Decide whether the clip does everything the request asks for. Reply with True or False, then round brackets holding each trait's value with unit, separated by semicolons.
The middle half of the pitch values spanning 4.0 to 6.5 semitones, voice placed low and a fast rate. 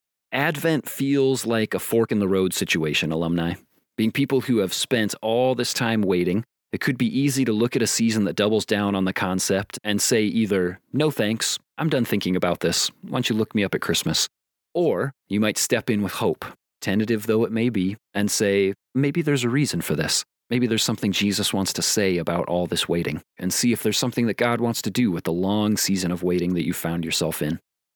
True (4.4 semitones; 105 Hz; 225 wpm)